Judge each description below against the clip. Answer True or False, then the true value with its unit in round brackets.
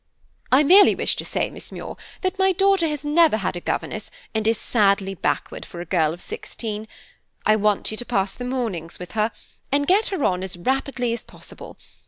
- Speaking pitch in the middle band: False (230 Hz)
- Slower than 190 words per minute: False (205 wpm)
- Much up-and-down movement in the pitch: True (7.2 semitones)